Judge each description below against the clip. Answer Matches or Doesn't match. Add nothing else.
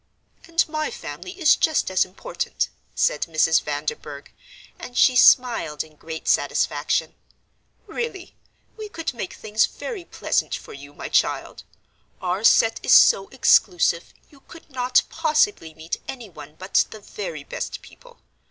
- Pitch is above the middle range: Matches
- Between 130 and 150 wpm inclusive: Matches